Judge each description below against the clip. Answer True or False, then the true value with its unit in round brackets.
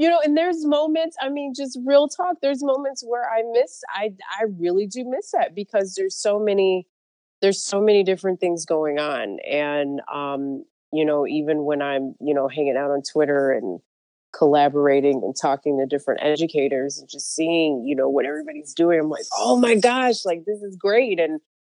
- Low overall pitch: False (170 Hz)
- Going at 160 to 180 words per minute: False (195 wpm)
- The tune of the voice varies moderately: False (7.7 semitones)